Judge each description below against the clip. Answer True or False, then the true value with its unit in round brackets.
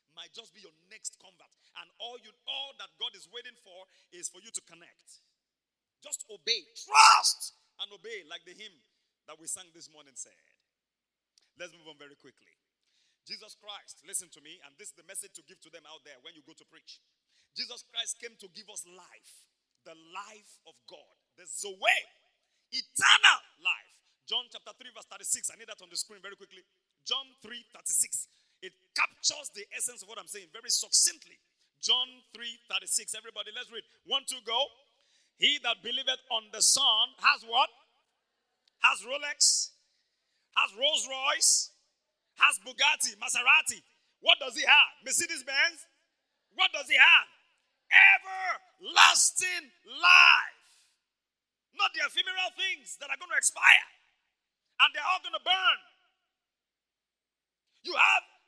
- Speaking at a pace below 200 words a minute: True (155 wpm)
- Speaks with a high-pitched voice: True (240 Hz)